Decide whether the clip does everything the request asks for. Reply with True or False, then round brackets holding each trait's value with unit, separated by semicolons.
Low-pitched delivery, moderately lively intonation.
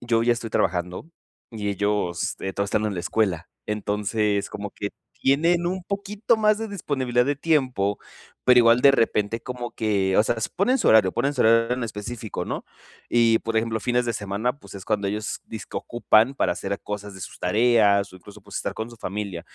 True (110 Hz; 3.4 semitones)